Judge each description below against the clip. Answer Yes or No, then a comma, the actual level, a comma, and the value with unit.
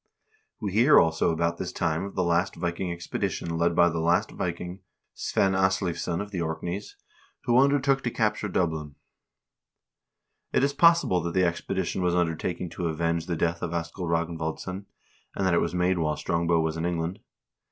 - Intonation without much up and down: Yes, narrow, 2.2 semitones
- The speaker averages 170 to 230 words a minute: Yes, average, 175 wpm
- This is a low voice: Yes, very low, 85 Hz